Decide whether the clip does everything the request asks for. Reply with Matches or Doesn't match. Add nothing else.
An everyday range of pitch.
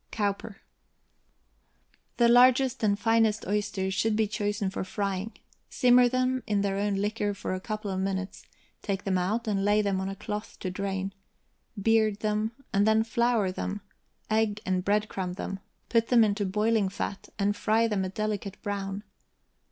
Doesn't match